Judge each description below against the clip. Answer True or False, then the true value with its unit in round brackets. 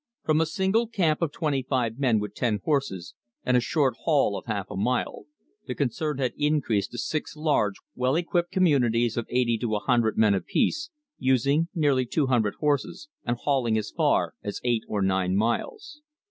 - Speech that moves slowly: False (185 wpm)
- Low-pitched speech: True (130 Hz)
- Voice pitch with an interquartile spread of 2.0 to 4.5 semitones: False (5.4 semitones)